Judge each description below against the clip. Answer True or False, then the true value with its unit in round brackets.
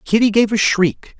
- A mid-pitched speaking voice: False (205 Hz)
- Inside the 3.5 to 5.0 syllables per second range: True (4.6 syllables/s)